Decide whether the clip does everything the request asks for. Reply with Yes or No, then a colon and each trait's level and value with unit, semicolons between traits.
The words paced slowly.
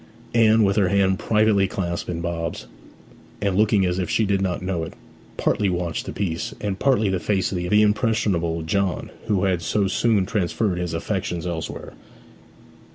No: average, 170 wpm